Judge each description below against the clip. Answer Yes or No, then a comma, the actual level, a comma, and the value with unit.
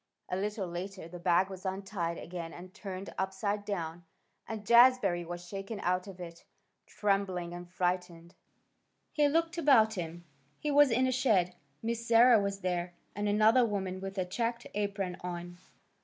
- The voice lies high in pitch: Yes, high, 195 Hz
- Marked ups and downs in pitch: No, average, 3.5 semitones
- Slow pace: No, average, 160 wpm